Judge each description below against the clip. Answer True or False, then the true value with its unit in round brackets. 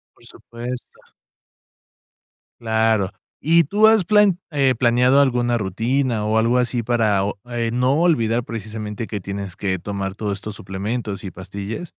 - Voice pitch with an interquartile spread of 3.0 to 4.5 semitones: True (3.7 semitones)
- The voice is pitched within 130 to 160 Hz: False (115 Hz)